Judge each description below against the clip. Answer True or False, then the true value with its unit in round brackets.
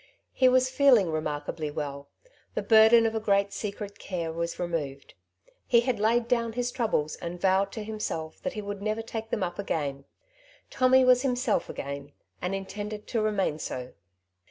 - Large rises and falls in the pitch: True (5.8 semitones)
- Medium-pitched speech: False (205 Hz)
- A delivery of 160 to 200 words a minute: True (170 wpm)